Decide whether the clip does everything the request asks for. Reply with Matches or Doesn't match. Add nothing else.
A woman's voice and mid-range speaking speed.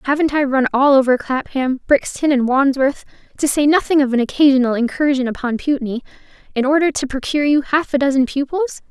Matches